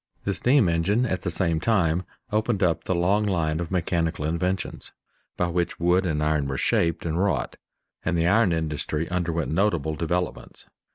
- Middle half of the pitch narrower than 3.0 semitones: Yes, narrow, 2.6 semitones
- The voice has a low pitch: Yes, very low, 85 Hz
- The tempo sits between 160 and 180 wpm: Yes, average, 170 wpm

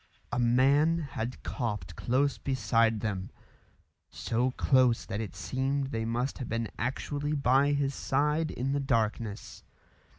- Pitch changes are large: No, average, 3.6 semitones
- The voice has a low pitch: Yes, low, 130 Hz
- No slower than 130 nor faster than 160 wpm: Yes, slow, 135 wpm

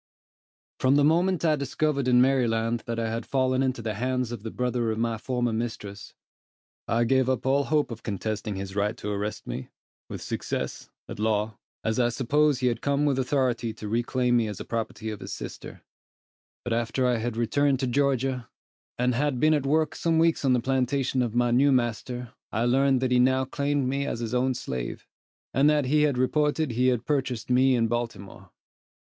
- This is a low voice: Yes, low, 125 Hz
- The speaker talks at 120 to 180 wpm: No, average, 200 wpm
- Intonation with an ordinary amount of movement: Yes, average, 3.0 semitones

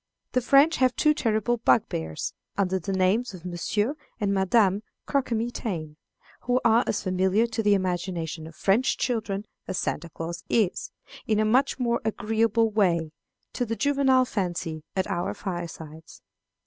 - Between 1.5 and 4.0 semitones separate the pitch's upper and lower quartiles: No, average, 4.6 semitones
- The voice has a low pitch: No, high, 205 Hz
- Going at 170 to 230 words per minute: No, average, 150 wpm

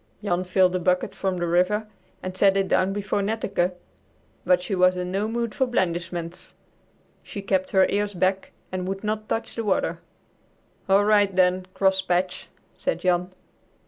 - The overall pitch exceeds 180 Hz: Yes, high, 190 Hz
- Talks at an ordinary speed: Yes, average, 165 wpm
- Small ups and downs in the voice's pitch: Yes, narrow, 2.0 semitones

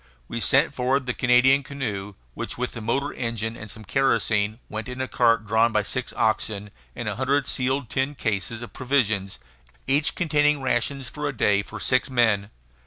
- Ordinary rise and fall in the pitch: Yes, average, 3.8 semitones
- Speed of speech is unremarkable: Yes, average, 180 wpm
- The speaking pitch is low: Yes, low, 120 Hz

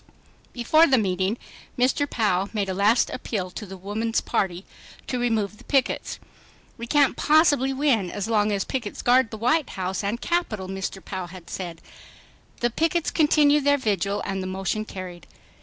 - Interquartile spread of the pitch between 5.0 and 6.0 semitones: Yes, wide, 5.4 semitones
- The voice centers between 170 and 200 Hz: No, high, 215 Hz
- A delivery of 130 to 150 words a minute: No, average, 170 wpm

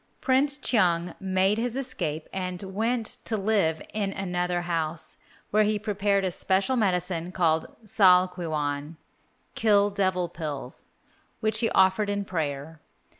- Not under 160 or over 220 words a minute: No, slow, 135 wpm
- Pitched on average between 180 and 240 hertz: Yes, high, 190 Hz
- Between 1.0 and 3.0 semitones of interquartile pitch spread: No, average, 3.7 semitones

